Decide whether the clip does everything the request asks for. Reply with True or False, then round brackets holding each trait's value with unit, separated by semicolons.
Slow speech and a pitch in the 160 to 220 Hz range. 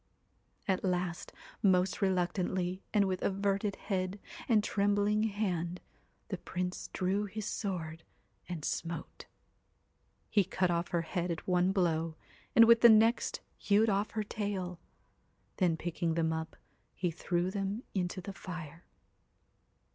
True (130 wpm; 185 Hz)